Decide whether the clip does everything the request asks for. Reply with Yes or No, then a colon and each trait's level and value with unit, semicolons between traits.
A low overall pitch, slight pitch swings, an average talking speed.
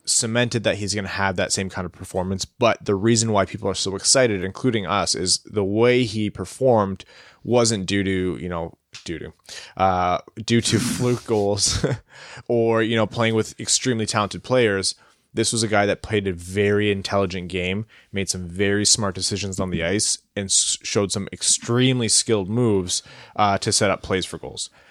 No: low, 100 Hz; average, 3.1 semitones; average, 190 wpm